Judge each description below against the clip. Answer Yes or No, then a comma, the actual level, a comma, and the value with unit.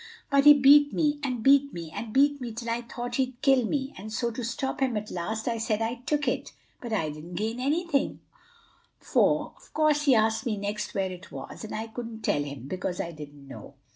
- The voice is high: Yes, high, 230 Hz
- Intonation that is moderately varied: Yes, average, 5.0 semitones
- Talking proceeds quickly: Yes, fast, 220 wpm